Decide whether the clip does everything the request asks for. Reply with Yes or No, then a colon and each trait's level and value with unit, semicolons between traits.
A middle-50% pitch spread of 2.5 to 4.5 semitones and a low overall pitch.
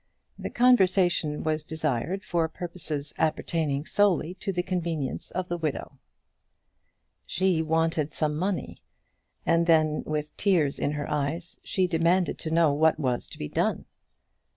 No: average, 2.9 semitones; medium, 160 Hz